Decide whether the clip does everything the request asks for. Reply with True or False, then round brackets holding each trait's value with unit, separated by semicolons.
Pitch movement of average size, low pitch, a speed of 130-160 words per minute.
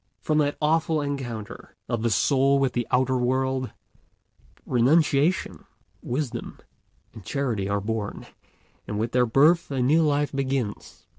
True (3.5 semitones; 130 Hz; 135 wpm)